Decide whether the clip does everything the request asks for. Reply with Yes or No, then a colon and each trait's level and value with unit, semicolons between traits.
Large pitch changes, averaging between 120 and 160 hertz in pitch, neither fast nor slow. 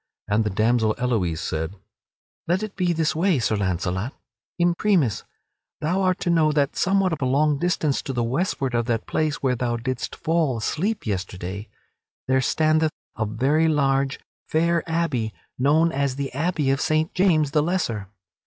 Yes: wide, 5.9 semitones; medium, 140 Hz; average, 165 wpm